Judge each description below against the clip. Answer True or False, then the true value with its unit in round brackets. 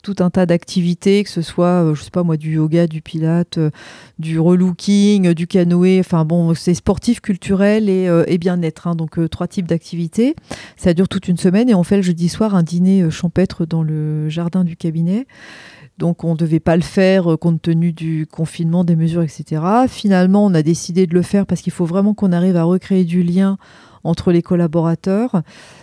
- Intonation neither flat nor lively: False (2.3 semitones)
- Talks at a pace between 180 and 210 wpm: True (200 wpm)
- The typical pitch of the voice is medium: True (175 Hz)